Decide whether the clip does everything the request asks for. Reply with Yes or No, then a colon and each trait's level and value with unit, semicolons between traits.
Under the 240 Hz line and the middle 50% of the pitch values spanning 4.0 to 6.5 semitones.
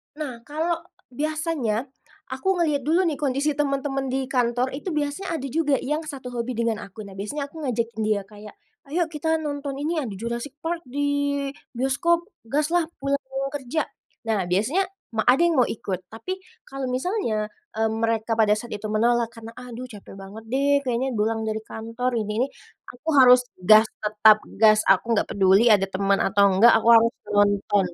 No: high, 245 Hz; average, 4.8 semitones